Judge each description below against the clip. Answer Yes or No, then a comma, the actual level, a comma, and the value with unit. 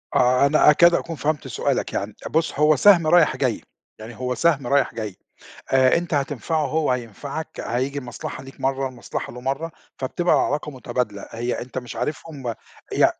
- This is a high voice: No, low, 135 Hz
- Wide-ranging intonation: No, average, 3.7 semitones